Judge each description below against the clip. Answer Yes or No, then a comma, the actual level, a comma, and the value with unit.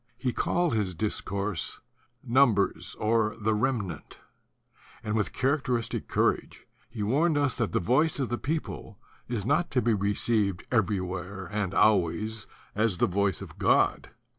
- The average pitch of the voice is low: Yes, low, 110 Hz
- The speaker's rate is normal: Yes, average, 150 wpm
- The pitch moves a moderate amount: Yes, average, 4.0 semitones